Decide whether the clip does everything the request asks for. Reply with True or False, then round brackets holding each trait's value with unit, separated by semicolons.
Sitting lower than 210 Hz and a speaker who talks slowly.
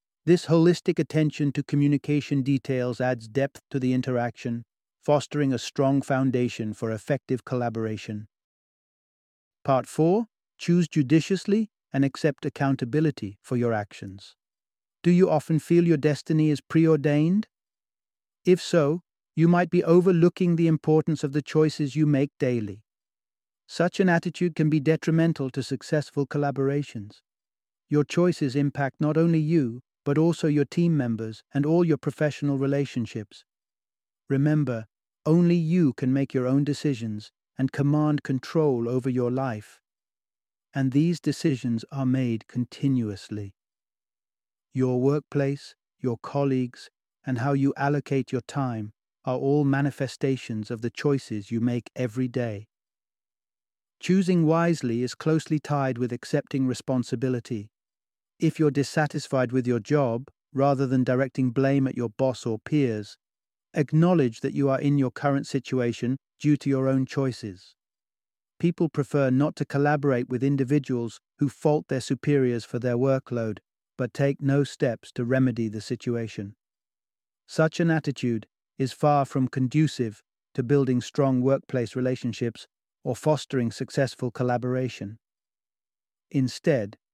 True (135 Hz; 130 wpm)